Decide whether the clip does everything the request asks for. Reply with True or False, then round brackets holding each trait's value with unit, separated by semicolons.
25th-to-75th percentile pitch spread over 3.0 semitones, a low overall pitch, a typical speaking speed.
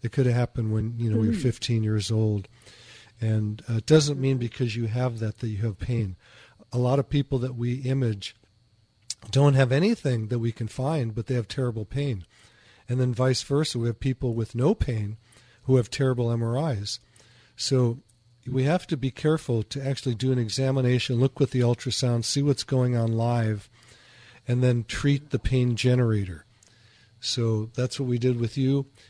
False (2.4 semitones; 120 Hz; 190 wpm)